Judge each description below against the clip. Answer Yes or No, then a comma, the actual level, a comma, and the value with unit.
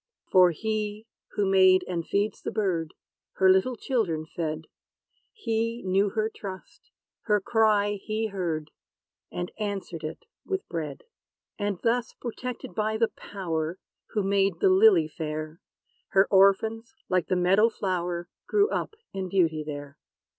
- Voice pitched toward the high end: Yes, high, 195 Hz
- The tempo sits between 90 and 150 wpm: Yes, average, 140 wpm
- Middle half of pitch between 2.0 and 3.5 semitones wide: No, average, 4.1 semitones